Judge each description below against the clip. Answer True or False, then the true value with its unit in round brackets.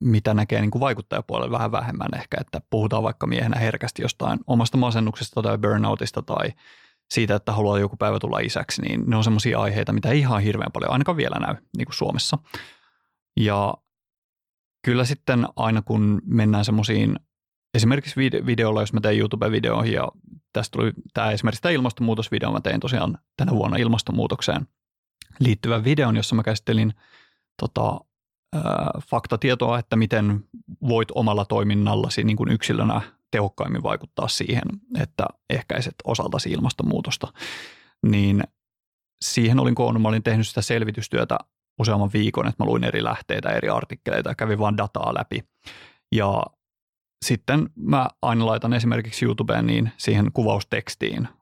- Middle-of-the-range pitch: False (110 Hz)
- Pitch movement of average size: False (2.1 semitones)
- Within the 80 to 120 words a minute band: False (140 wpm)